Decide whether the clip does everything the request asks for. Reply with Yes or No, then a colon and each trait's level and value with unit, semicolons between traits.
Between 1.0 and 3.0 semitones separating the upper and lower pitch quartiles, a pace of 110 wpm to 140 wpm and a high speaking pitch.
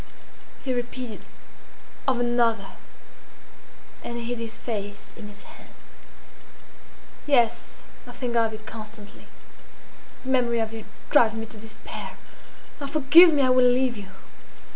Yes: narrow, 2.4 semitones; slow, 135 wpm; high, 235 Hz